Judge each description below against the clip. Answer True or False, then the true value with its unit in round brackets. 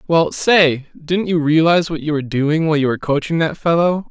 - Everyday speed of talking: False (220 wpm)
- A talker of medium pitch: True (160 Hz)